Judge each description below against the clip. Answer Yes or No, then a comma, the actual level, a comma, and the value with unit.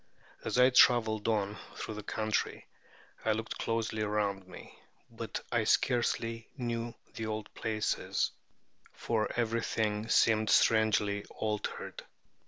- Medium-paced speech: No, slow, 115 wpm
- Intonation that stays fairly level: Yes, narrow, 1.4 semitones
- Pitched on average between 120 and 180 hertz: No, low, 110 Hz